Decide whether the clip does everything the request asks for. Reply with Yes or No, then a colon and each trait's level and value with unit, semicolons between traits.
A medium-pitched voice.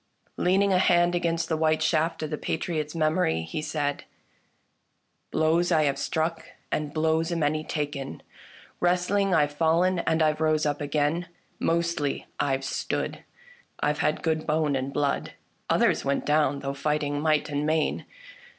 Yes: medium, 155 Hz